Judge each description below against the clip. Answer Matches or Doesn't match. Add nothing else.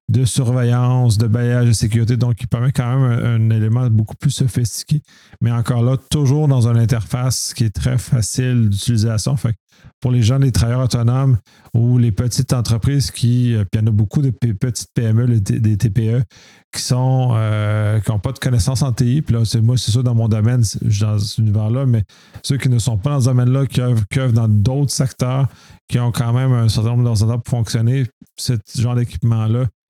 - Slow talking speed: Doesn't match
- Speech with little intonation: Matches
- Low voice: Matches